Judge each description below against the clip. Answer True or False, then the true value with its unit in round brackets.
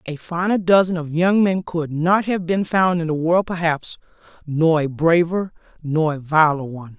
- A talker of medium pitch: True (165 Hz)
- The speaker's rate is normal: True (190 wpm)